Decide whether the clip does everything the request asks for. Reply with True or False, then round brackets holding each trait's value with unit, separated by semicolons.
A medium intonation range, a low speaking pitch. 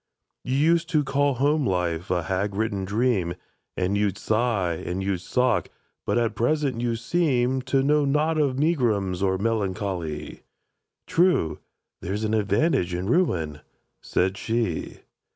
False (6.5 semitones; 110 Hz)